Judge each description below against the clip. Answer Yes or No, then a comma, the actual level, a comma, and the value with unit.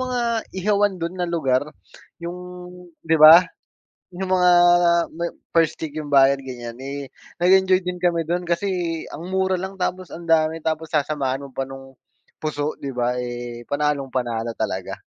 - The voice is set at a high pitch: No, medium, 160 Hz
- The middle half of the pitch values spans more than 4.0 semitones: Yes, average, 5.1 semitones